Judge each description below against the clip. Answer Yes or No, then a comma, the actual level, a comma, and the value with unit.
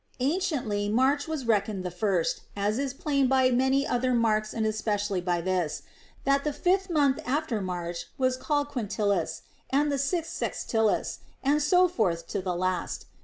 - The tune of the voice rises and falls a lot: Yes, wide, 5.8 semitones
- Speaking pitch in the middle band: No, high, 235 Hz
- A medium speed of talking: Yes, average, 165 wpm